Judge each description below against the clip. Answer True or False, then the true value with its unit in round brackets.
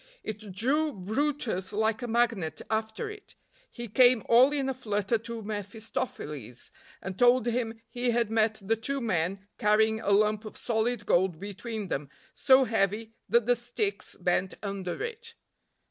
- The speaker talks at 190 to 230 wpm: False (155 wpm)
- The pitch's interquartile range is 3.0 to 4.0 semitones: True (3.3 semitones)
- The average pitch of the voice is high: True (220 Hz)